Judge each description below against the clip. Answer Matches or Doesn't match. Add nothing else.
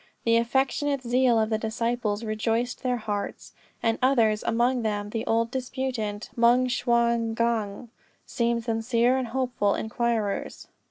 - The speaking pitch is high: Matches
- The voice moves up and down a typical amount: Doesn't match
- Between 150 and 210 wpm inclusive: Doesn't match